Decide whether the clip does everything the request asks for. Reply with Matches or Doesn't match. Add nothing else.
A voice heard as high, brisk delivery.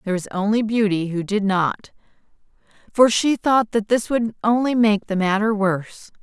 Doesn't match